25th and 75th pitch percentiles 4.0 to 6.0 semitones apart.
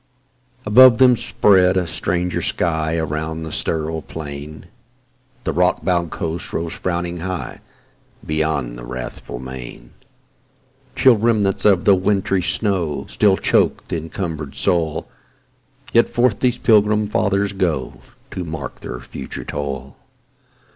Yes: average, 4.6 semitones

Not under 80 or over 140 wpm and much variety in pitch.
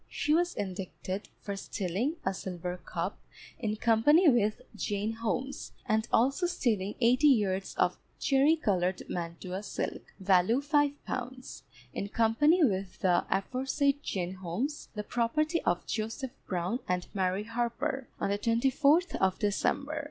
Yes: slow, 135 wpm; wide, 6.2 semitones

